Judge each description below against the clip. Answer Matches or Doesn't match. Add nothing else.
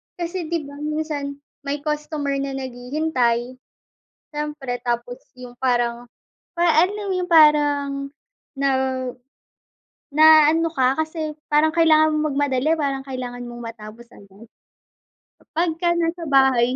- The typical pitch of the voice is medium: Doesn't match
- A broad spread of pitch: Doesn't match